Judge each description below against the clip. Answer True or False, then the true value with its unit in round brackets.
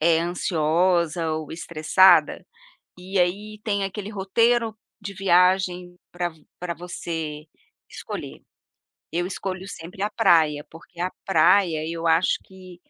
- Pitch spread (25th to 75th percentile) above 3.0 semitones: False (2.7 semitones)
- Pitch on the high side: False (180 Hz)